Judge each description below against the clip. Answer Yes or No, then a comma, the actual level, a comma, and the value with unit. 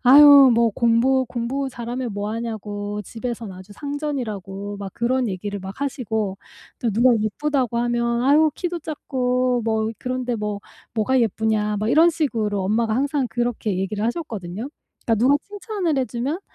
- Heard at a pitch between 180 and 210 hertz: No, high, 235 Hz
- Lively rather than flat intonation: No, average, 3.9 semitones